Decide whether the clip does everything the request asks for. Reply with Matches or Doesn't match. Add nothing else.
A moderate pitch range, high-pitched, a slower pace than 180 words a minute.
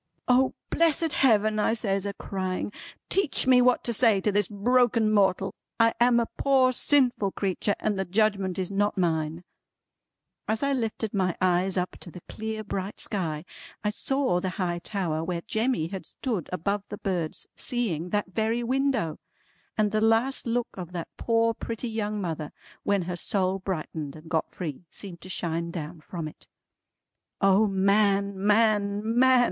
Matches